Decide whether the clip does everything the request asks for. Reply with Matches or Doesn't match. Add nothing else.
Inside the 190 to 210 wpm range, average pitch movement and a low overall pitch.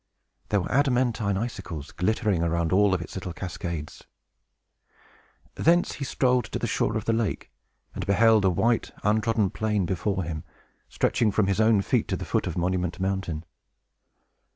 Doesn't match